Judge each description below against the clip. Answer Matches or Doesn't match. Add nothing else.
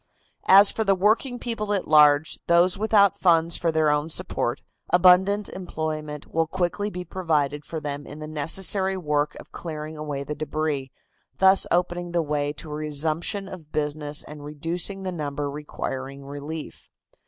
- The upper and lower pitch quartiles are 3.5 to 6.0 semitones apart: Matches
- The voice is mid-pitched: Matches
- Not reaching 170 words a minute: Matches